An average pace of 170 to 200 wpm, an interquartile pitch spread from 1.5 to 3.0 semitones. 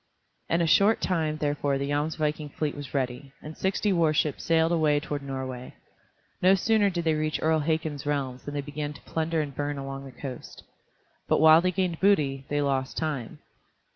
Yes: average, 185 wpm; narrow, 2.6 semitones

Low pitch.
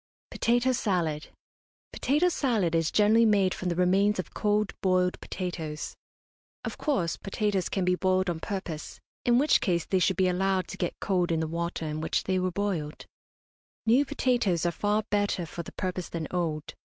No: medium, 185 Hz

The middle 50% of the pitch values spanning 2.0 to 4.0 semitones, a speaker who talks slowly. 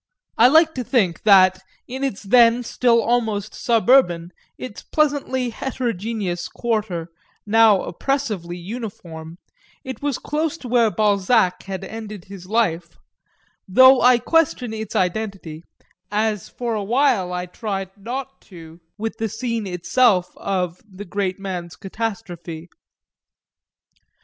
No: average, 4.8 semitones; slow, 125 wpm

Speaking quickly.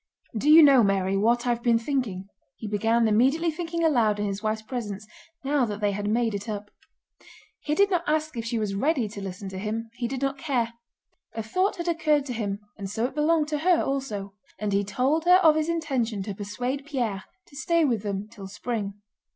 Yes: fast, 215 wpm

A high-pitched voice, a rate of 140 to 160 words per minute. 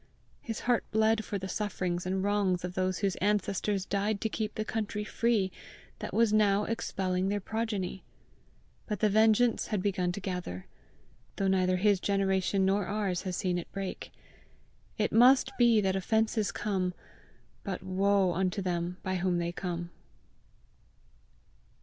Yes: high, 195 Hz; average, 150 wpm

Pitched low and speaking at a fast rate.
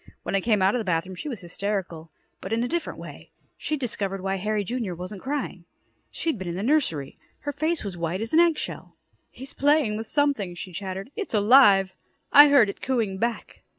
No: high, 210 Hz; fast, 210 wpm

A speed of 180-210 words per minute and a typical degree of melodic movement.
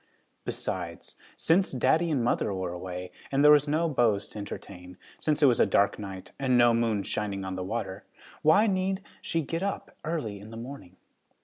No: average, 190 wpm; wide, 7.9 semitones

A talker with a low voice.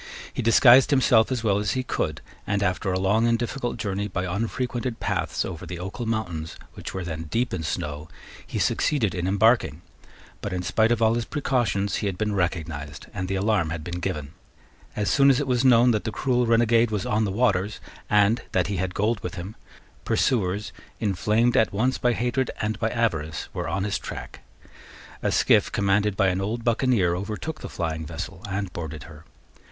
Yes: low, 105 Hz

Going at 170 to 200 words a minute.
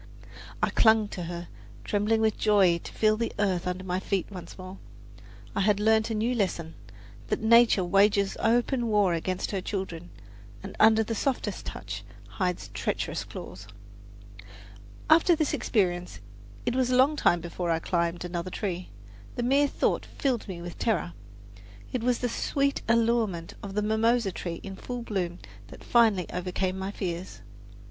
No: average, 160 wpm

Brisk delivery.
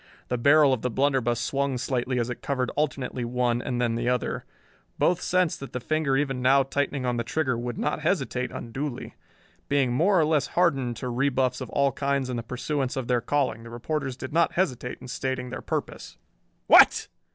No: average, 195 wpm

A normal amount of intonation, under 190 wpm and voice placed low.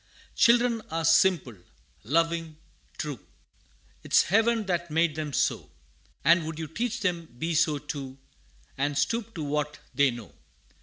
No: average, 3.9 semitones; average, 140 wpm; medium, 165 Hz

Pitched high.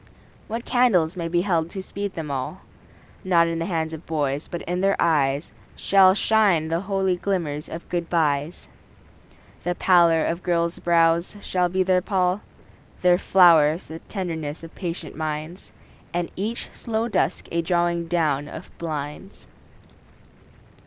No: medium, 170 Hz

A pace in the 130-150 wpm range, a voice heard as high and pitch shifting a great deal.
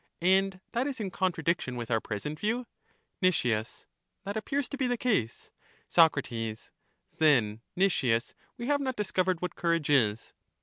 No: average, 145 wpm; medium, 180 Hz; wide, 9.0 semitones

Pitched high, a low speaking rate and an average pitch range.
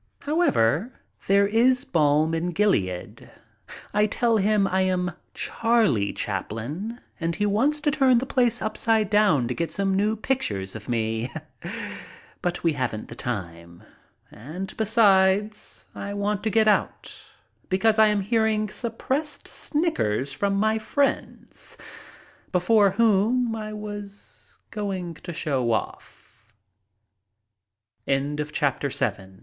No: high, 200 Hz; slow, 120 wpm; wide, 5.9 semitones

